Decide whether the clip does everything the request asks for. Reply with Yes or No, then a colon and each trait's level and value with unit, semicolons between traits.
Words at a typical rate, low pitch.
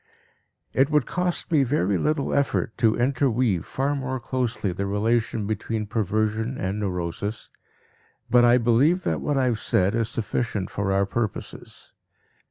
Yes: average, 150 wpm; low, 115 Hz